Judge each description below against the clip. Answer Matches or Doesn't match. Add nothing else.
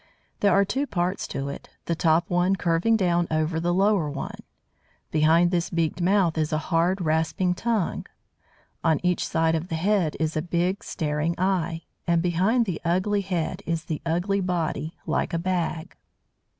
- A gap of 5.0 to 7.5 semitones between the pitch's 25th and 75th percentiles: Doesn't match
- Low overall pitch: Doesn't match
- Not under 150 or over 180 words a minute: Matches